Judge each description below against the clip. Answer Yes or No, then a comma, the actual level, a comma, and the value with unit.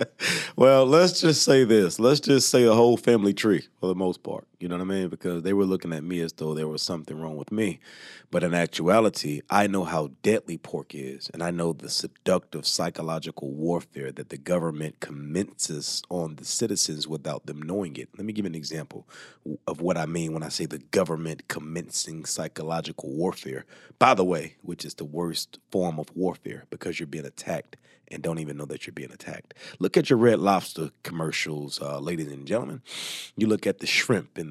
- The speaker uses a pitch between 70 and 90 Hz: Yes, very low, 85 Hz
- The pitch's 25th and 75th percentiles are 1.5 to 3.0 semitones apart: No, average, 3.5 semitones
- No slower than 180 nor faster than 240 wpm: Yes, fast, 205 wpm